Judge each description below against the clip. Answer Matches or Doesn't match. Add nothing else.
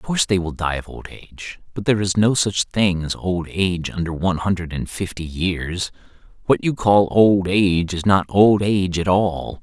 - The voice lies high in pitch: Doesn't match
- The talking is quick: Matches